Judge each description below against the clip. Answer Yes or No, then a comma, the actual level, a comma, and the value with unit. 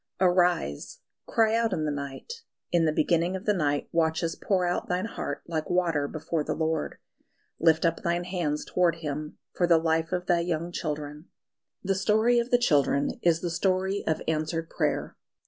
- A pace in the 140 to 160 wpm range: No, average, 180 wpm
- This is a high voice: No, medium, 170 Hz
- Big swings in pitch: No, narrow, 2.6 semitones